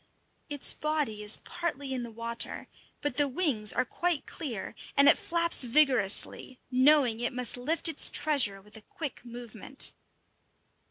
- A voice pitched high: Yes, very high, 255 Hz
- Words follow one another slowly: No, average, 155 wpm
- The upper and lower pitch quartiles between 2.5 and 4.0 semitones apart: No, average, 4.4 semitones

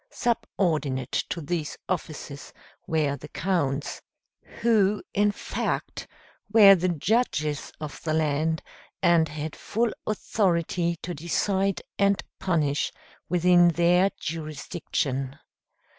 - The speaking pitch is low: No, medium, 170 Hz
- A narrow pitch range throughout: No, average, 4.2 semitones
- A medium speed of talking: No, slow, 100 wpm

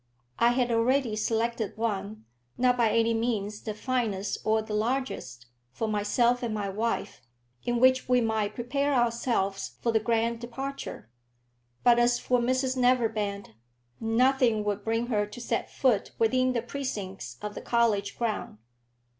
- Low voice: No, high, 230 Hz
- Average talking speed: Yes, average, 150 wpm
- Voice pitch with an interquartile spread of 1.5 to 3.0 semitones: Yes, narrow, 2.6 semitones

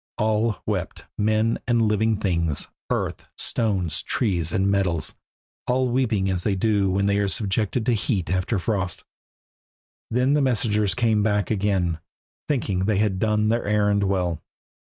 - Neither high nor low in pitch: No, low, 105 Hz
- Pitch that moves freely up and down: No, average, 2.7 semitones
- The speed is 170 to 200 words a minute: No, average, 150 wpm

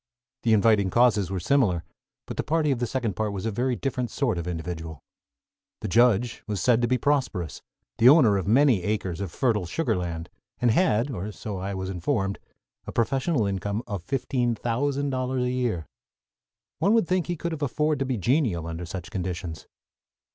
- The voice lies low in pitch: Yes, low, 115 Hz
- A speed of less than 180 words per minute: No, average, 190 wpm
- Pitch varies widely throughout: Yes, wide, 5.8 semitones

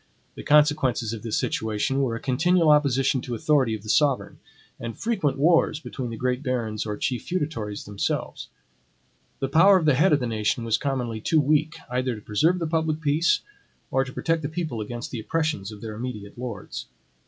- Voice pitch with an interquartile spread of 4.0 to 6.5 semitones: Yes, average, 5.0 semitones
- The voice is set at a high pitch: No, low, 130 Hz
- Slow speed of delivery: No, average, 190 wpm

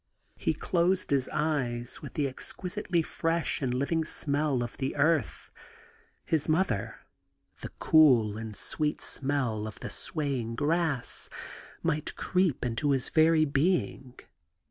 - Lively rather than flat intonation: No, average, 4.1 semitones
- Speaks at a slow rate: Yes, slow, 125 wpm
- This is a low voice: No, medium, 145 Hz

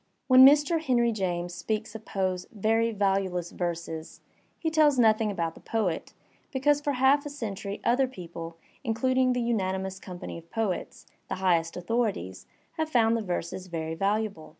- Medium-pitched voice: No, high, 210 Hz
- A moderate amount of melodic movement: No, wide, 5.7 semitones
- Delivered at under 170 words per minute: Yes, average, 160 wpm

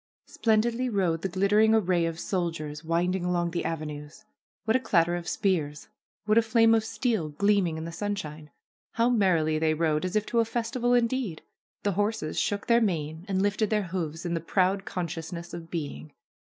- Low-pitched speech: No, medium, 180 Hz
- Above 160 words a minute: Yes, average, 190 wpm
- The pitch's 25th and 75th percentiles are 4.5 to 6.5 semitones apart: Yes, average, 4.8 semitones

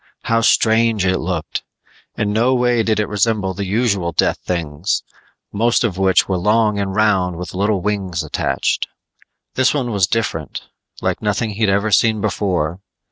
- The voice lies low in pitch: Yes, low, 105 Hz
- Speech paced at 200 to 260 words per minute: No, average, 160 wpm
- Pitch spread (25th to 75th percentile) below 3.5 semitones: Yes, average, 3.1 semitones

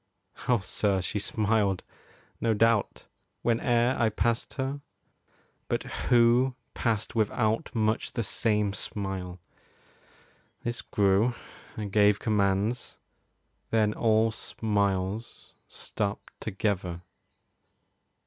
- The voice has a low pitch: Yes, low, 110 Hz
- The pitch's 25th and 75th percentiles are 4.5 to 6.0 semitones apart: No, narrow, 2.5 semitones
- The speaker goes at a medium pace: No, slow, 90 wpm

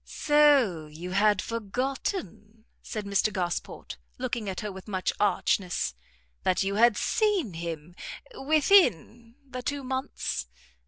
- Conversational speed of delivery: No, slow, 120 wpm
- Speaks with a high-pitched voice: Yes, high, 215 Hz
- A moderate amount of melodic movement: No, wide, 5.9 semitones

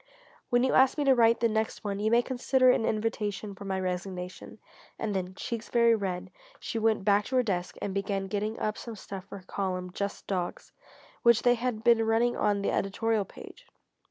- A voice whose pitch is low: No, high, 215 Hz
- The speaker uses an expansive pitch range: No, average, 3.2 semitones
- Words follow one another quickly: Yes, fast, 210 wpm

